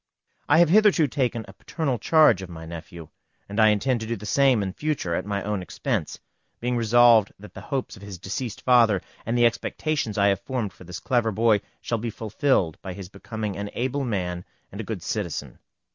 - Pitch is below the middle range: Yes, low, 110 Hz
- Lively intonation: No, average, 4.1 semitones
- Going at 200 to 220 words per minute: Yes, fast, 205 wpm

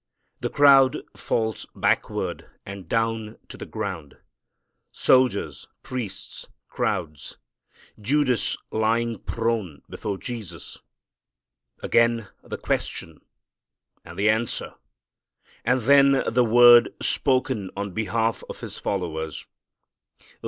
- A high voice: No, low, 115 Hz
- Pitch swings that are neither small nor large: Yes, average, 3.8 semitones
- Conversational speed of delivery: No, slow, 95 wpm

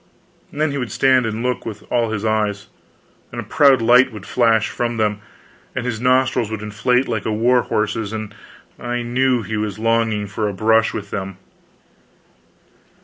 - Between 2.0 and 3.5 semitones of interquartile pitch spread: Yes, narrow, 2.5 semitones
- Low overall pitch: Yes, low, 115 Hz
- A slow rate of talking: No, average, 175 wpm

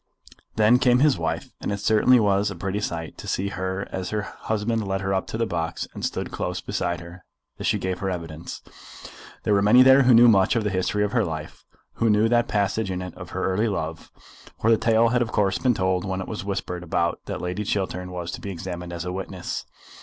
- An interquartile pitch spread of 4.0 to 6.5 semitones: No, average, 3.4 semitones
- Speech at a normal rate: No, fast, 235 wpm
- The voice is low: Yes, very low, 95 Hz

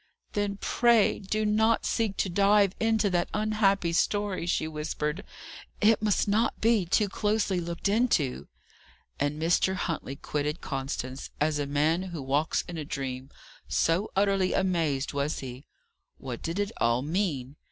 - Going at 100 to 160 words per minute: Yes, average, 150 wpm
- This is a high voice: No, medium, 175 Hz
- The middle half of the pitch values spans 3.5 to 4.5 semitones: No, wide, 5.6 semitones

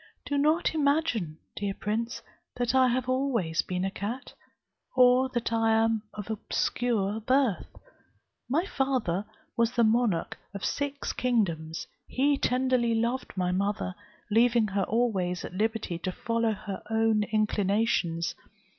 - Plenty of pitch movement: No, average, 4.1 semitones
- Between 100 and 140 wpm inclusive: Yes, slow, 135 wpm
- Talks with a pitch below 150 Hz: No, high, 225 Hz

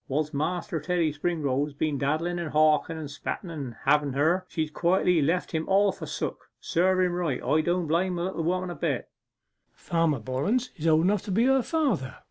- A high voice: No, medium, 165 Hz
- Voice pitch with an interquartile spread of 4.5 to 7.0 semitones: No, average, 3.4 semitones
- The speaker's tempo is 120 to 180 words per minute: No, average, 195 wpm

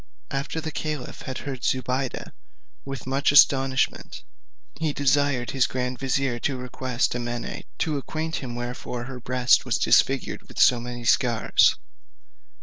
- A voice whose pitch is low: Yes, low, 130 Hz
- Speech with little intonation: Yes, narrow, 2.2 semitones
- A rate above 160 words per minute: No, average, 140 wpm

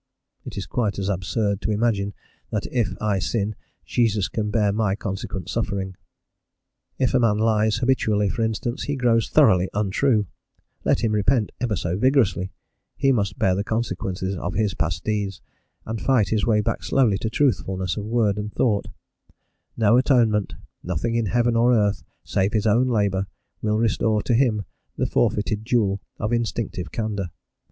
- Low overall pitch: Yes, low, 105 Hz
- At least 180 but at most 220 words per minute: No, average, 165 wpm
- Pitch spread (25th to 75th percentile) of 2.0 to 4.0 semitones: Yes, average, 2.7 semitones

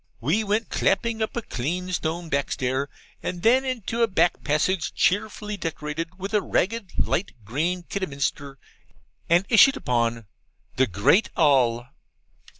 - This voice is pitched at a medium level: Yes, medium, 175 Hz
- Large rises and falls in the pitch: Yes, wide, 6.8 semitones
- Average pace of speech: No, slow, 130 wpm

